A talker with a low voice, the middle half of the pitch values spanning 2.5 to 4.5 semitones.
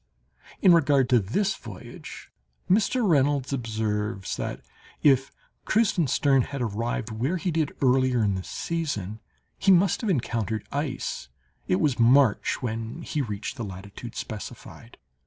No: low, 125 Hz; wide, 5.5 semitones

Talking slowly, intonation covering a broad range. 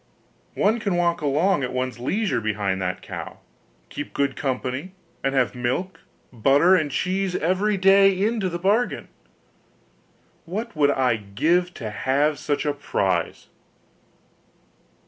Yes: slow, 130 wpm; wide, 6.7 semitones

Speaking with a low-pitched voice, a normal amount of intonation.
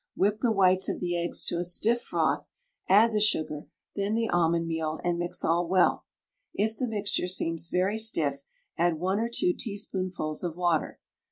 No: medium, 180 Hz; average, 3.9 semitones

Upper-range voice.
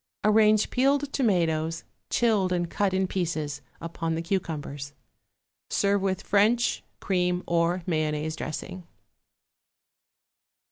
No: medium, 180 Hz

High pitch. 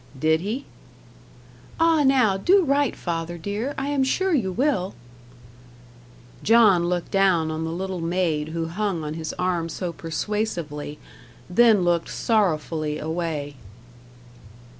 No: medium, 180 Hz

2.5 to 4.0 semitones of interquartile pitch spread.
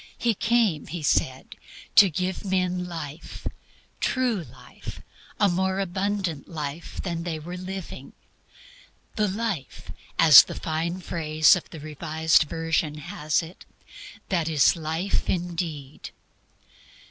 Yes: average, 3.3 semitones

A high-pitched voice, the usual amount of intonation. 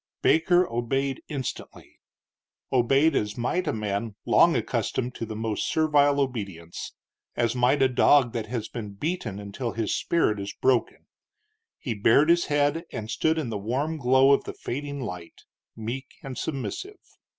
No: low, 125 Hz; average, 4.6 semitones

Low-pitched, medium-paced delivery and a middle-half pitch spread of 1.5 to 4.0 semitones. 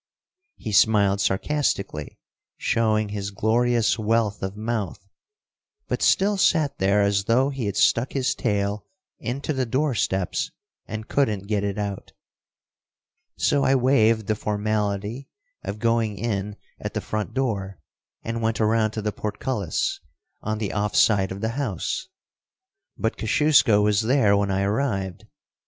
Yes: low, 110 Hz; average, 145 wpm; average, 2.8 semitones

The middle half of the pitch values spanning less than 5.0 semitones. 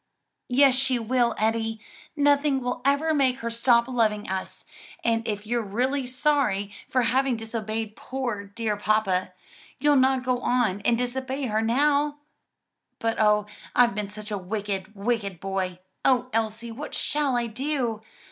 Yes: average, 3.6 semitones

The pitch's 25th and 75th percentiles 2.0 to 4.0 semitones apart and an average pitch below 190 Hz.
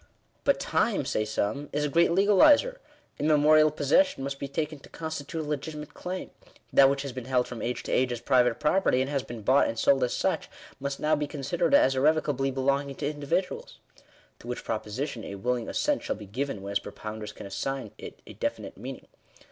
Yes: average, 3.7 semitones; medium, 140 Hz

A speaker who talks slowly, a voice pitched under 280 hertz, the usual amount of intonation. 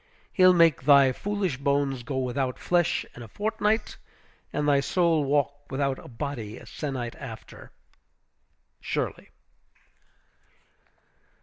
Yes: slow, 115 wpm; medium, 140 Hz; average, 4.2 semitones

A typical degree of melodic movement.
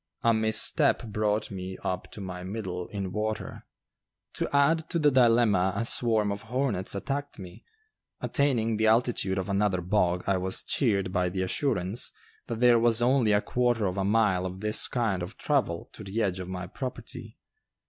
Yes: average, 4.0 semitones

